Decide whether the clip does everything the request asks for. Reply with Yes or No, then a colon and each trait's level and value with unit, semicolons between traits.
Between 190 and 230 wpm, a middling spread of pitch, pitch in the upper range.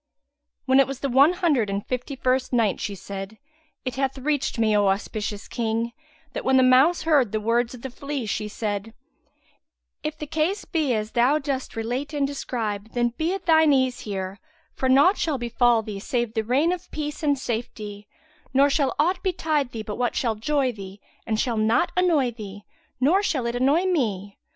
Yes: average, 195 wpm; average, 4.8 semitones; very high, 255 Hz